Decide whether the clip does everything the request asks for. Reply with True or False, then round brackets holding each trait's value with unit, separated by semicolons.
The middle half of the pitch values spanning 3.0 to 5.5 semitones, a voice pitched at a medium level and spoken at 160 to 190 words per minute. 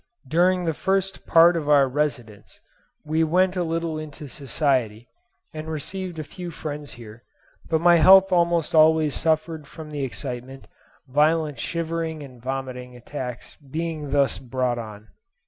False (3.9 semitones; 155 Hz; 145 wpm)